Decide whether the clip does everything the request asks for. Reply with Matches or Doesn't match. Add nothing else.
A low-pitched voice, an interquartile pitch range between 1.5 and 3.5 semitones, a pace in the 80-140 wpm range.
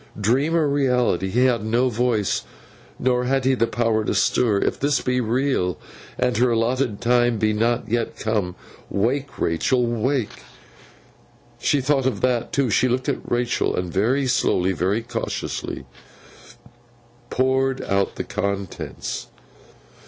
Matches